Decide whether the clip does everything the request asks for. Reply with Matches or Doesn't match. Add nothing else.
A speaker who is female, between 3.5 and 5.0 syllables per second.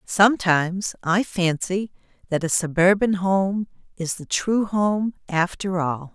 Matches